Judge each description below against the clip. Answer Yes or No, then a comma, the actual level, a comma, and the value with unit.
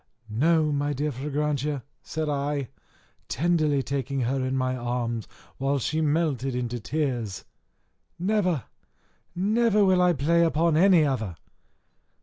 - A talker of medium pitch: Yes, medium, 145 Hz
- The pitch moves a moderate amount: Yes, average, 4.1 semitones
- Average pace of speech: No, slow, 125 wpm